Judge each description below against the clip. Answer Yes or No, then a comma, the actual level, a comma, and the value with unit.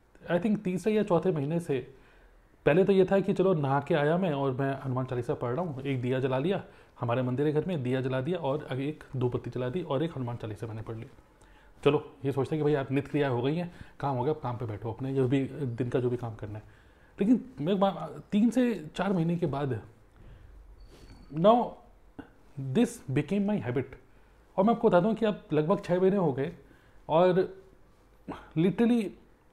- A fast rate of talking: Yes, fast, 215 wpm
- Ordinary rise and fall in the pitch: No, wide, 6.4 semitones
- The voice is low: No, medium, 145 Hz